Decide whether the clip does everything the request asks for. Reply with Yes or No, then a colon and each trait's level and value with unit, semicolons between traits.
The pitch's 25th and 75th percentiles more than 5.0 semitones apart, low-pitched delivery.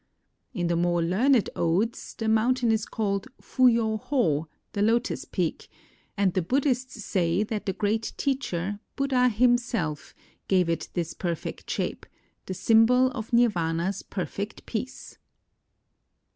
No: wide, 5.4 semitones; high, 215 Hz